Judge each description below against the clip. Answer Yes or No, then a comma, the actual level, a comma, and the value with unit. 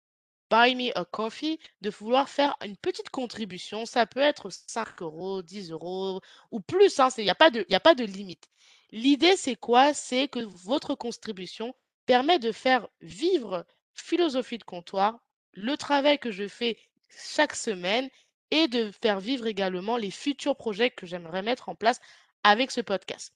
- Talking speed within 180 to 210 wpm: No, average, 165 wpm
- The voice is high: Yes, high, 235 Hz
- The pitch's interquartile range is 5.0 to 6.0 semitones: Yes, wide, 5.5 semitones